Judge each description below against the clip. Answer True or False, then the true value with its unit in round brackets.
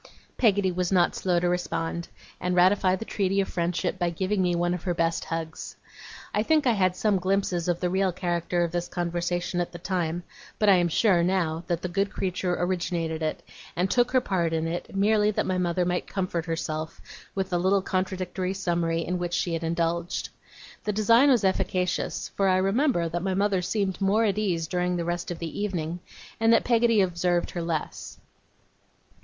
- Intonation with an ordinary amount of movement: False (2.2 semitones)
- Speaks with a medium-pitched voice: True (180 Hz)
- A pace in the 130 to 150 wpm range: False (195 wpm)